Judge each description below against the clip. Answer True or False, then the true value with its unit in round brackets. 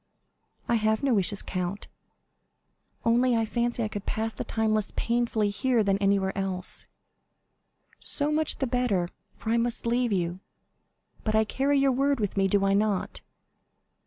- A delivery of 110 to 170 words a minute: True (160 wpm)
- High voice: True (220 Hz)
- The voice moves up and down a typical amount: True (3.4 semitones)